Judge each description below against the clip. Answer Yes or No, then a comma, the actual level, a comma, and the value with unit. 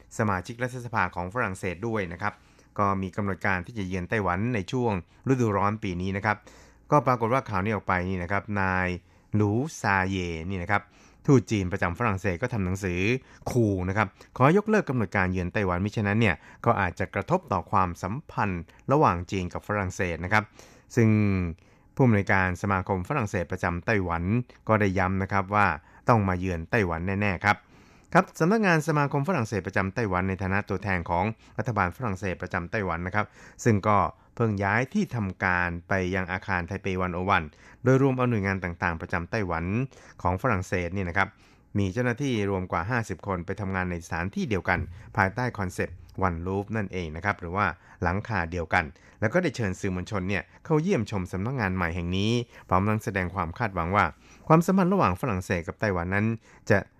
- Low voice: Yes, low, 100 Hz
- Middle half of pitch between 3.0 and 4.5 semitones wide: Yes, average, 3.5 semitones